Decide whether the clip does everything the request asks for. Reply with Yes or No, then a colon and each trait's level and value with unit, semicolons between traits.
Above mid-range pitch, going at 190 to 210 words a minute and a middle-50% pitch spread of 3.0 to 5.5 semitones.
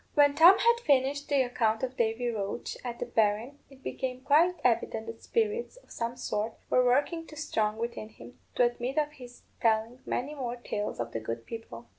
Yes: high, 245 Hz; average, 195 wpm; average, 4.3 semitones